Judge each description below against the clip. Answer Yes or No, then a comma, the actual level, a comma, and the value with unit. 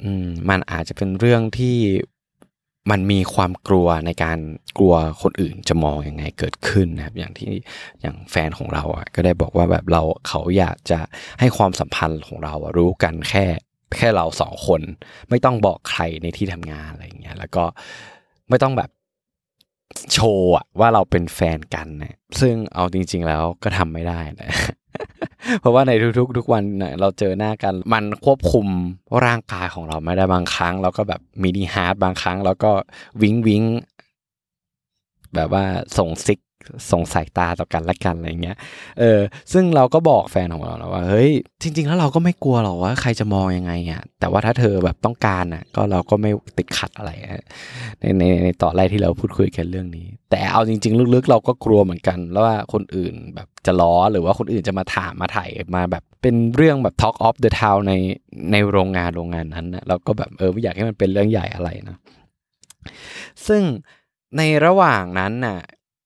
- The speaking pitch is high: No, very low, 95 Hz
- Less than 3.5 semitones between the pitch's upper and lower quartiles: No, average, 4.3 semitones